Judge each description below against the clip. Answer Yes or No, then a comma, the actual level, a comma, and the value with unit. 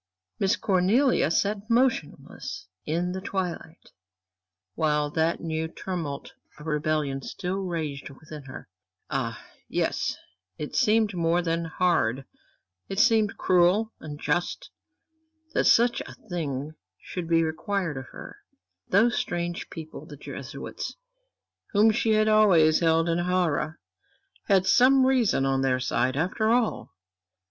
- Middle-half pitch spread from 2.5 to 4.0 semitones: No, average, 4.7 semitones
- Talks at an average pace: No, slow, 125 wpm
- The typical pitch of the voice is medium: Yes, medium, 170 Hz